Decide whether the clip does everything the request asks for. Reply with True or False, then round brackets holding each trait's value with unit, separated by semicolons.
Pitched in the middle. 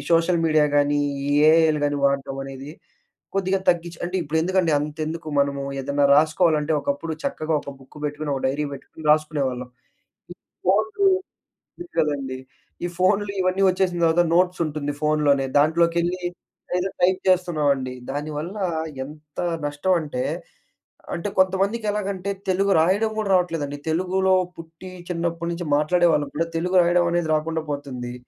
True (160 Hz)